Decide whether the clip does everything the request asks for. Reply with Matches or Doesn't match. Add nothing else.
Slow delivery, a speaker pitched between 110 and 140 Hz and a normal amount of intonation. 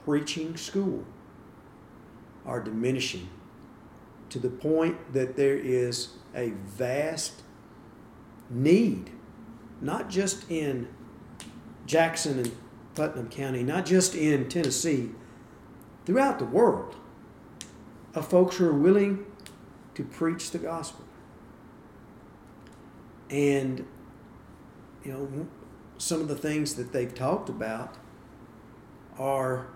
Matches